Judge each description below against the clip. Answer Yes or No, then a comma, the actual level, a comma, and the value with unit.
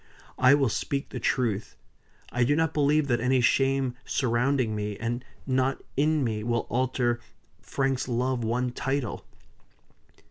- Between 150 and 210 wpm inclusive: No, average, 140 wpm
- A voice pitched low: Yes, low, 130 Hz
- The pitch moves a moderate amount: No, narrow, 2.3 semitones